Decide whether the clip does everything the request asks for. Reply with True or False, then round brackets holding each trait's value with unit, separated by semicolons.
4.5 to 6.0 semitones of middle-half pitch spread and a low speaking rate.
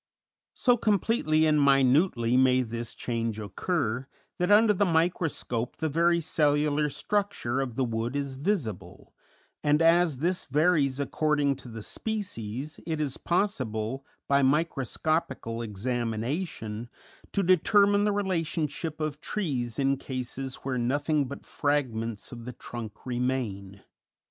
True (5.4 semitones; 125 wpm)